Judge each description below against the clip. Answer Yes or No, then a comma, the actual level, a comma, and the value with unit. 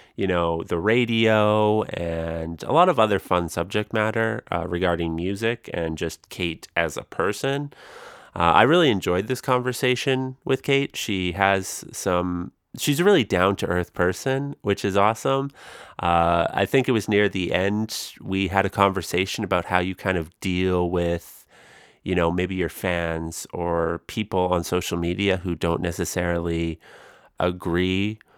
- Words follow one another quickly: No, average, 160 wpm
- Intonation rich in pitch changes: No, average, 3.8 semitones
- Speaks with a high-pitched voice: No, very low, 95 Hz